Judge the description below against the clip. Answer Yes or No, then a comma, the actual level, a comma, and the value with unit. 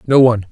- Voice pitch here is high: No, low, 115 Hz